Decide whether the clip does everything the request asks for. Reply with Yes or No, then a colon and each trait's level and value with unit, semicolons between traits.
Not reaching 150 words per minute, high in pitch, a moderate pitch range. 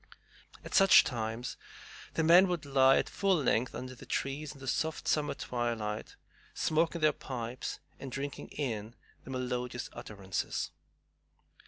No: average, 140 wpm; low, 130 Hz; average, 4.2 semitones